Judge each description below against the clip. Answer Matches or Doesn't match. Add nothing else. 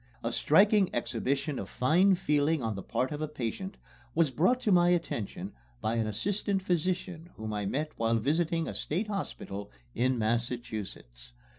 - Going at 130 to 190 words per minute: Matches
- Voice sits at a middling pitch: Matches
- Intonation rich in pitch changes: Matches